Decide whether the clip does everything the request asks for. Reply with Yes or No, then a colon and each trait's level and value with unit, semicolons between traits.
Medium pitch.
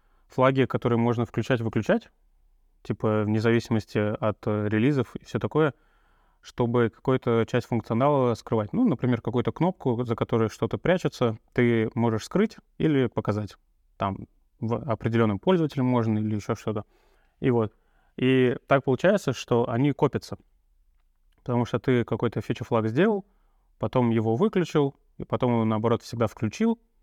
No: low, 120 Hz